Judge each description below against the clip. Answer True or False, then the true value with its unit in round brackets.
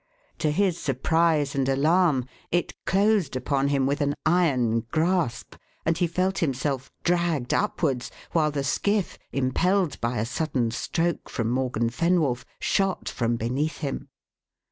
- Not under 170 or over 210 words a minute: False (140 wpm)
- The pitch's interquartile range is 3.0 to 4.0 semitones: False (5.1 semitones)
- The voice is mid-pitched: True (150 Hz)